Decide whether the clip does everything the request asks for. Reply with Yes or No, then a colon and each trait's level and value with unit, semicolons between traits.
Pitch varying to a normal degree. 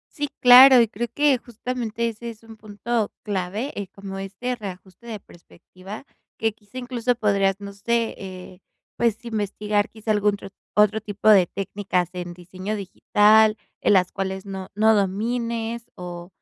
Yes: average, 3.1 semitones